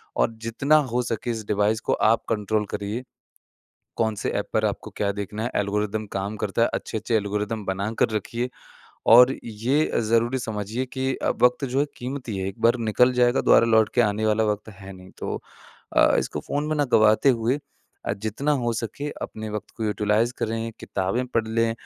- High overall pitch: No, low, 110 Hz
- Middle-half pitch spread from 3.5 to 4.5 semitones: No, average, 2.7 semitones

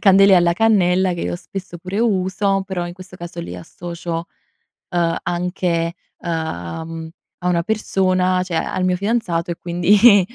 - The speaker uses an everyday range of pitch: No, narrow, 2.1 semitones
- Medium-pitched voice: Yes, medium, 180 Hz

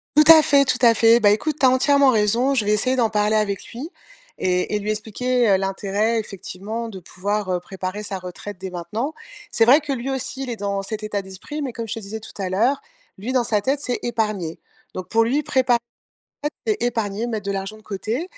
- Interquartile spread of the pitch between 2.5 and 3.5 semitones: No, average, 4.0 semitones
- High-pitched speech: Yes, high, 220 Hz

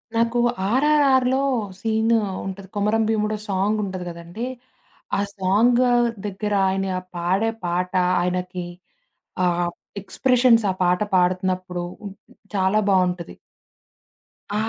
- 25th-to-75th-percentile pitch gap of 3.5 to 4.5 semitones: Yes, average, 3.8 semitones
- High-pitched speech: Yes, high, 195 Hz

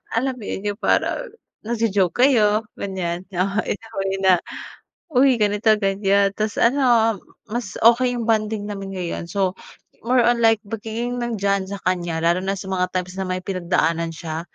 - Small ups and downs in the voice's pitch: No, average, 3.6 semitones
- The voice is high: Yes, high, 200 Hz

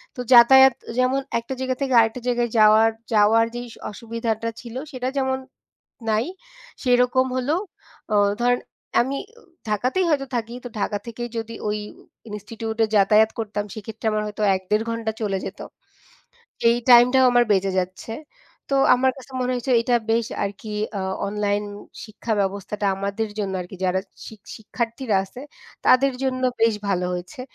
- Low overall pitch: No, high, 230 Hz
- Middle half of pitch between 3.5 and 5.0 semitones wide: No, average, 3.1 semitones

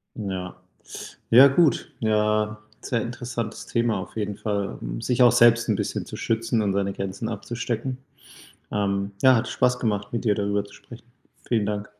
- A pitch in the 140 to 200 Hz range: No, low, 110 Hz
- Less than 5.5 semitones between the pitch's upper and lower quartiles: Yes, average, 2.7 semitones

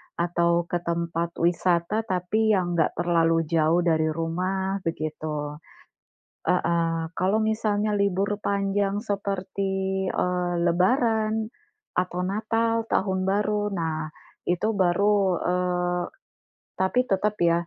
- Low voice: No, medium, 185 Hz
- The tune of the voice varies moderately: Yes, average, 3.2 semitones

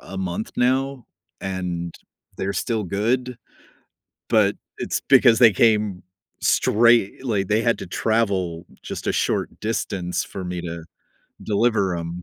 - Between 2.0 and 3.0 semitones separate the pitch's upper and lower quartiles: No, average, 4.3 semitones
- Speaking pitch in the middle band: No, low, 105 Hz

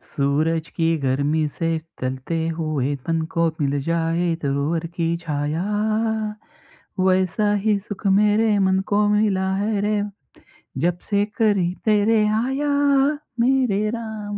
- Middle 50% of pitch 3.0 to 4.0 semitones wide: No, average, 4.8 semitones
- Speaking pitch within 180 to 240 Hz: Yes, medium, 185 Hz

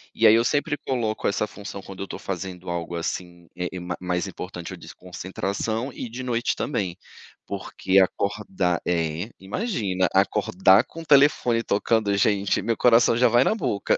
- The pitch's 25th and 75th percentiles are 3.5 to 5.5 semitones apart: Yes, average, 4.4 semitones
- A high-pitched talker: No, low, 100 Hz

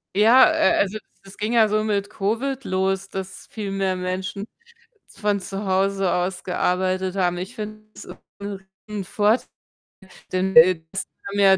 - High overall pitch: Yes, high, 195 Hz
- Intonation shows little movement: Yes, narrow, 2.1 semitones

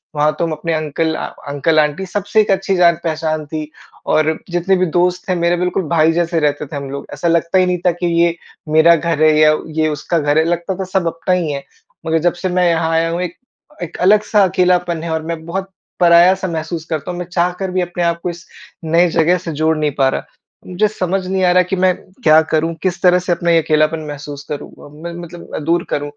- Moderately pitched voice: Yes, medium, 170 Hz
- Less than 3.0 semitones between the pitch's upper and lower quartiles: Yes, narrow, 2.4 semitones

